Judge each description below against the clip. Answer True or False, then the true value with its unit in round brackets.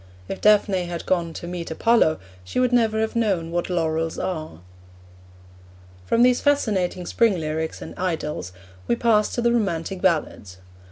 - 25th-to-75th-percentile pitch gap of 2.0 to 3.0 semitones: False (5.2 semitones)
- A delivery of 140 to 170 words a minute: True (155 wpm)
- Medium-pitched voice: True (180 Hz)